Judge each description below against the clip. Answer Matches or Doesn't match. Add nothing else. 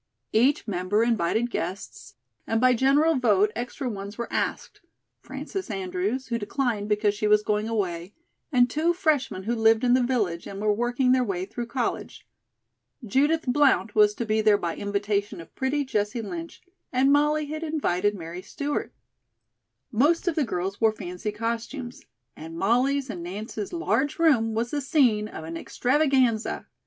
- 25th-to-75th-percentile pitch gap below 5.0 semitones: Matches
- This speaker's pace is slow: Doesn't match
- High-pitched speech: Matches